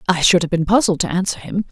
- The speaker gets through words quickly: Yes, fast, 280 wpm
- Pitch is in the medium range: Yes, medium, 180 Hz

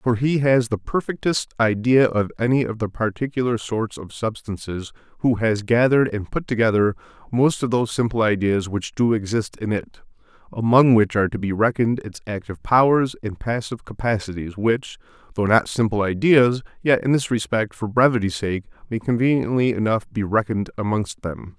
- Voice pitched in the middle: No, low, 110 Hz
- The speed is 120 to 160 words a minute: No, average, 170 wpm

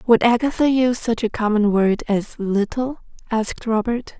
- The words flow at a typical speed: Yes, average, 160 wpm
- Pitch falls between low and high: No, high, 225 Hz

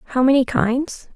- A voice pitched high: Yes, very high, 260 Hz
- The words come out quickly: No, average, 155 wpm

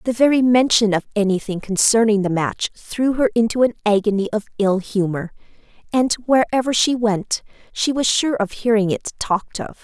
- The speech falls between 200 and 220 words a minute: No, average, 170 wpm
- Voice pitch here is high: Yes, high, 220 Hz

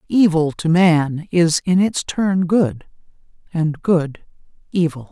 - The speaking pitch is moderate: Yes, medium, 165 Hz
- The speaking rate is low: Yes, slow, 130 wpm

